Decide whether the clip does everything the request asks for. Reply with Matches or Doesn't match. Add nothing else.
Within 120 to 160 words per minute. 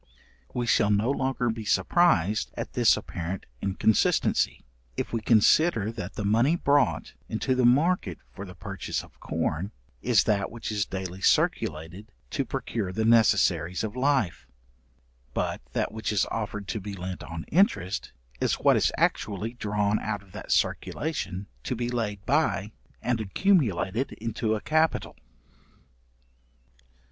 Matches